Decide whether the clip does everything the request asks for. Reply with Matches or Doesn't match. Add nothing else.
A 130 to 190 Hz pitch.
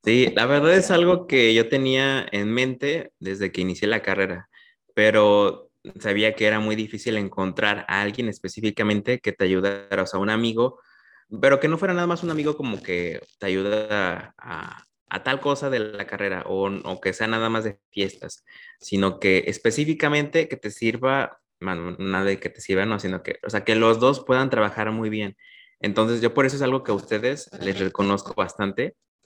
Doesn't match